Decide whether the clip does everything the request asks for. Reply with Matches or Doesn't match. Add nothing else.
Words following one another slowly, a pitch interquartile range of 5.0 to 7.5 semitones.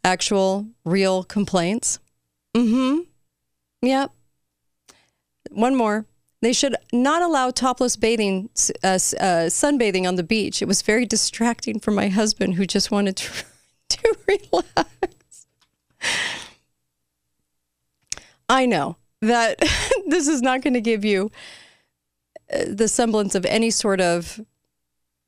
Matches